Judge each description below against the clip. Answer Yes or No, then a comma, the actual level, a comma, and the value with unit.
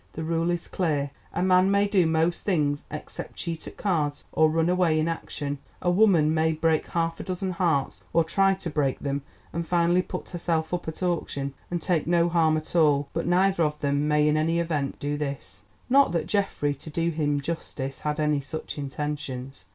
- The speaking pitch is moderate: Yes, medium, 160 Hz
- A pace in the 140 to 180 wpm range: No, average, 195 wpm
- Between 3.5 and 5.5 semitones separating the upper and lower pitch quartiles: No, average, 2.8 semitones